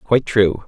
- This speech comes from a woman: No, male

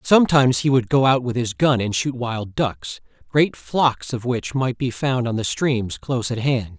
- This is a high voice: No, low, 130 Hz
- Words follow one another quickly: Yes, fast, 230 wpm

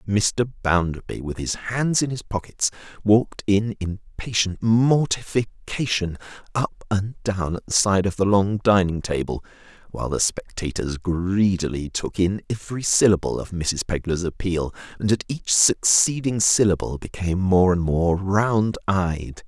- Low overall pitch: Yes, low, 100 Hz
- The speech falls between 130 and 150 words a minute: Yes, average, 140 wpm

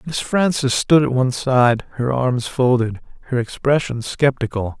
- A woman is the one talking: No, male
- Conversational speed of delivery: Yes, average, 150 wpm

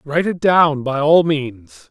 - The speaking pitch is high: No, medium, 145 Hz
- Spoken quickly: No, average, 190 wpm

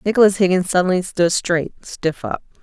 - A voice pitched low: No, medium, 185 Hz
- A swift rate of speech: No, average, 160 wpm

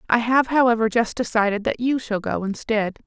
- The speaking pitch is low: No, high, 230 Hz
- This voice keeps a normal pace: Yes, average, 195 wpm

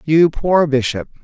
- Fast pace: No, average, 145 wpm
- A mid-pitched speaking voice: Yes, medium, 150 Hz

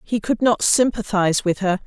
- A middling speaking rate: Yes, average, 195 wpm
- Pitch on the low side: No, high, 205 Hz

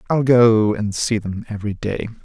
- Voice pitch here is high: No, low, 110 Hz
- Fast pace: No, average, 190 wpm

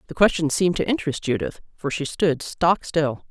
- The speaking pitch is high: No, medium, 165 Hz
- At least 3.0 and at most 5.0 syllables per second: No, 5.4 syllables/s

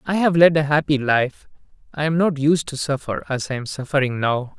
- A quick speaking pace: Yes, fast, 220 wpm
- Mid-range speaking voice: Yes, medium, 145 Hz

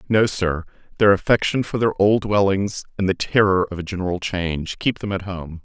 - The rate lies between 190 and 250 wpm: Yes, average, 200 wpm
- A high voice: No, very low, 95 Hz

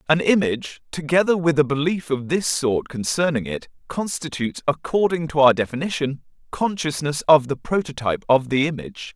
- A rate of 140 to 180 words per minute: Yes, average, 150 wpm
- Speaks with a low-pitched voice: No, medium, 150 Hz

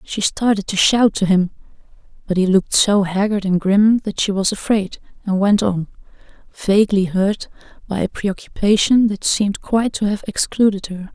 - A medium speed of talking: Yes, average, 170 wpm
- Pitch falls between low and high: No, high, 200 Hz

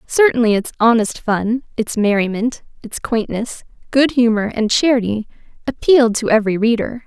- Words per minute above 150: No, slow, 135 wpm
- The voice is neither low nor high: No, high, 230 Hz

